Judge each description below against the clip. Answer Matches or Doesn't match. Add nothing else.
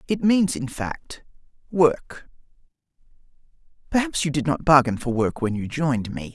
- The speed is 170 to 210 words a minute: Doesn't match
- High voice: Doesn't match